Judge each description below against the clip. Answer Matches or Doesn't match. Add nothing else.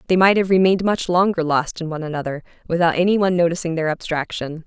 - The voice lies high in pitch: Doesn't match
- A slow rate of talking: Doesn't match